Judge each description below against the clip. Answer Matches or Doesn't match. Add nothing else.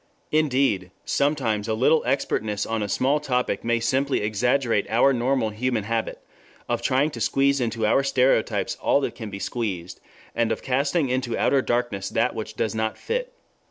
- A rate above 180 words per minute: Doesn't match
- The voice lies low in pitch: Matches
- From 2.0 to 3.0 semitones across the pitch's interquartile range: Doesn't match